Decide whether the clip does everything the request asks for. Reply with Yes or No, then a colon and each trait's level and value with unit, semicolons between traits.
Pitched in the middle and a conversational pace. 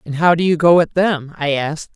No: medium, 160 Hz; fast, 275 wpm